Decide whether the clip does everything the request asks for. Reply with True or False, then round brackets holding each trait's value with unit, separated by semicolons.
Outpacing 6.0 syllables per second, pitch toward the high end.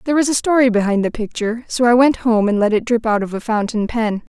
True (6.4 syllables/s; 230 Hz)